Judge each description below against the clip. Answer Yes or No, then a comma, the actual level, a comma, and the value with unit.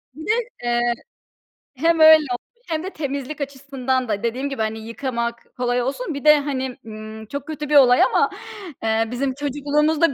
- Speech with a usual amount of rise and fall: Yes, average, 3.7 semitones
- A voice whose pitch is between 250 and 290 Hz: Yes, very high, 270 Hz